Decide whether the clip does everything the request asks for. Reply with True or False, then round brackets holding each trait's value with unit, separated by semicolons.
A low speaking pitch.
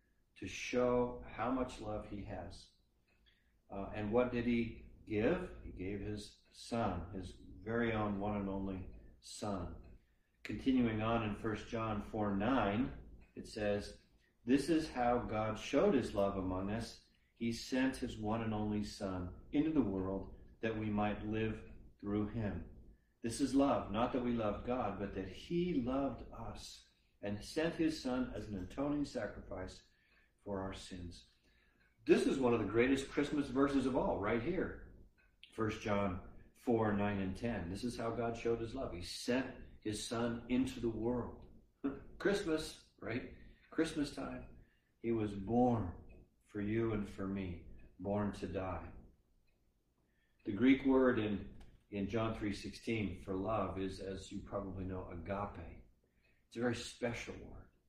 True (105 Hz)